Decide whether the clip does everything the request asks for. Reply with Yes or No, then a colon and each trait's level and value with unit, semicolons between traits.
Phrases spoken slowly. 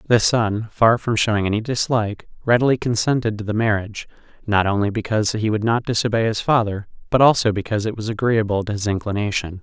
No: average, 185 wpm